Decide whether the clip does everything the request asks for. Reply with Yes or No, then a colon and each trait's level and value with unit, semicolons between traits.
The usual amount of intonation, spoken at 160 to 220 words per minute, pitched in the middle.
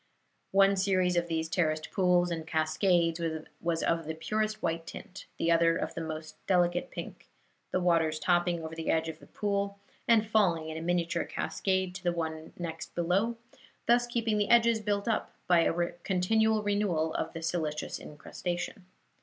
Yes: average, 3.5 semitones; average, 170 wpm; medium, 175 Hz